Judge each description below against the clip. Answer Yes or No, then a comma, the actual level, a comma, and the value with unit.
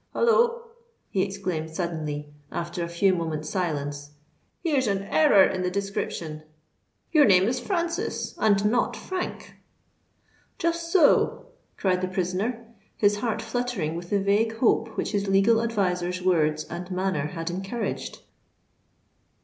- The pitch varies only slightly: No, average, 5.1 semitones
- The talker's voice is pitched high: Yes, high, 195 Hz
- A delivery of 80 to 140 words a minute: Yes, slow, 135 wpm